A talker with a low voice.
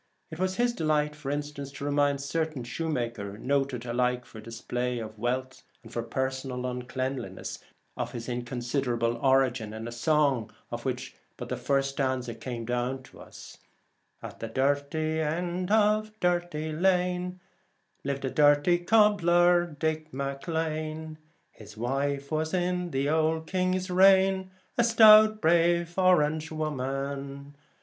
No: medium, 145 Hz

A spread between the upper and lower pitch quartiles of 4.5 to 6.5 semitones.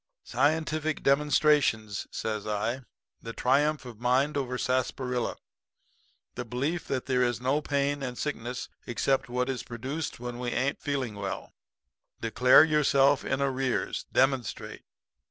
No: average, 2.7 semitones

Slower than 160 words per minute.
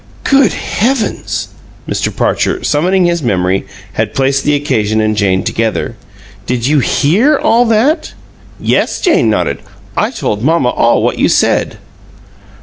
Yes: average, 140 wpm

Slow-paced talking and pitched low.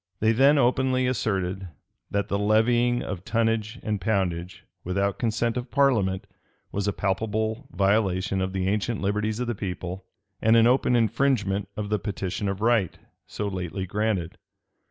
No: average, 155 wpm; low, 105 Hz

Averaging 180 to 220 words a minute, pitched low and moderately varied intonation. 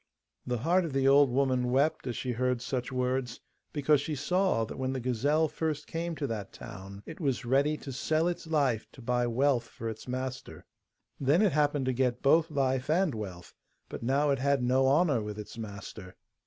Yes: average, 200 wpm; low, 130 Hz; average, 3.3 semitones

